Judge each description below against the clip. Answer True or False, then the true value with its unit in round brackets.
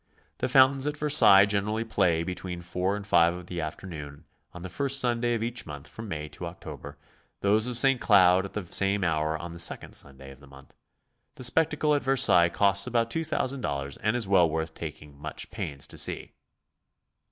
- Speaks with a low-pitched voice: True (95 Hz)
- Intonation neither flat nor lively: False (6.6 semitones)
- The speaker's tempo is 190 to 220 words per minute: True (195 wpm)